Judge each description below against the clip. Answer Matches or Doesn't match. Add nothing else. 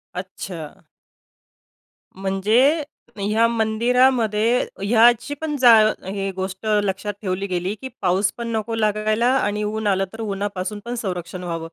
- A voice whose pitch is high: Matches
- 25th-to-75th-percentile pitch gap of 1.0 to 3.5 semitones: Matches